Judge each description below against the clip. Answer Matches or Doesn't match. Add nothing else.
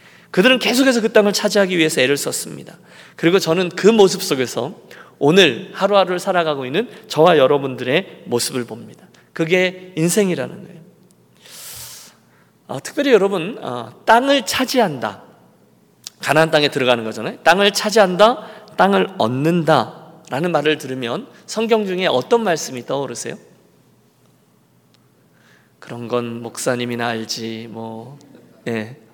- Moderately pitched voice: Matches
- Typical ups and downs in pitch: Doesn't match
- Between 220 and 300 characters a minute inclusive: Matches